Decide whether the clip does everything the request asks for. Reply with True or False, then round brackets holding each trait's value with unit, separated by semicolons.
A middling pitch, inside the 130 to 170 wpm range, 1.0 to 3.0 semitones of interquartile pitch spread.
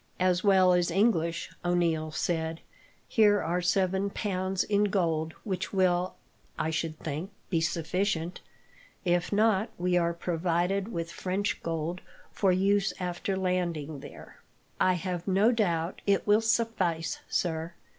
True (180 Hz; 135 wpm; 2.7 semitones)